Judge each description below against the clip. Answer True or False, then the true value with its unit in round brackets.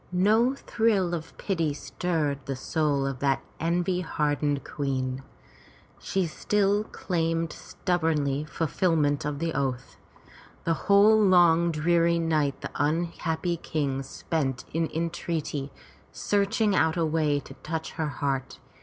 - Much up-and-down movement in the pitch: False (3.3 semitones)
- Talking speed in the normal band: False (125 wpm)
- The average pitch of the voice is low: False (160 Hz)